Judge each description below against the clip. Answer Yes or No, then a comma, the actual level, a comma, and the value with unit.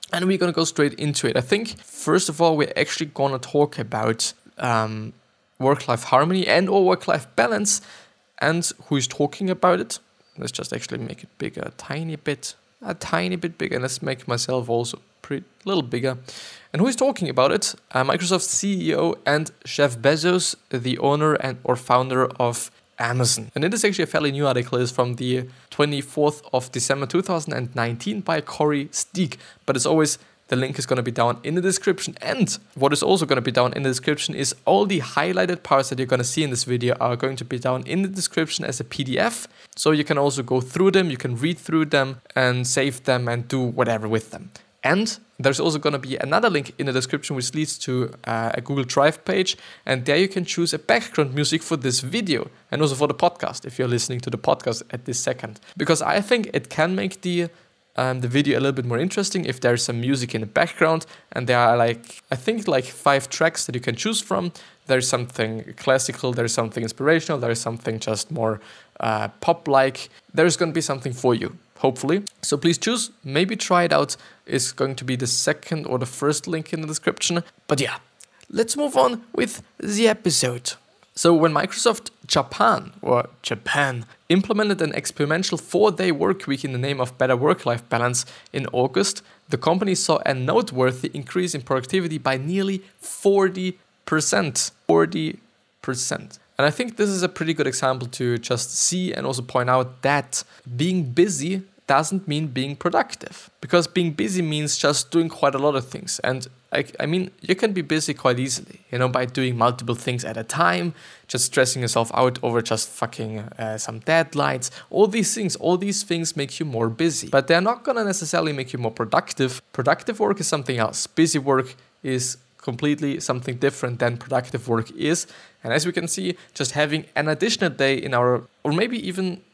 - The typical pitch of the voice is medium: Yes, medium, 145 Hz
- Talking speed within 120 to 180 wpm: No, average, 200 wpm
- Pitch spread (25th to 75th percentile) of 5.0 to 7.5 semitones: Yes, average, 5.3 semitones